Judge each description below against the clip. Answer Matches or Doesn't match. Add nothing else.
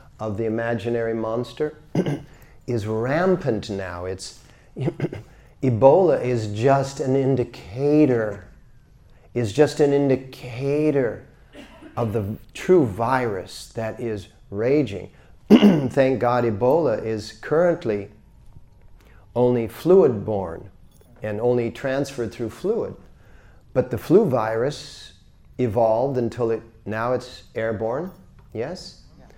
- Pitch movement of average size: Matches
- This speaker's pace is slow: Matches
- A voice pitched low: Matches